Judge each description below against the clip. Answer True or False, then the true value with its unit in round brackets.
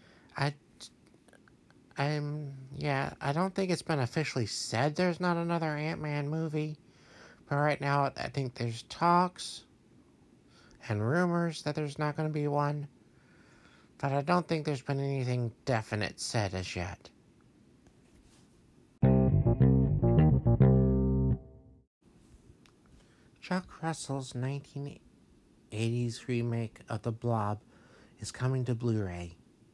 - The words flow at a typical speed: False (105 wpm)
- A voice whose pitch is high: False (135 Hz)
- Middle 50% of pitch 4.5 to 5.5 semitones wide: True (4.9 semitones)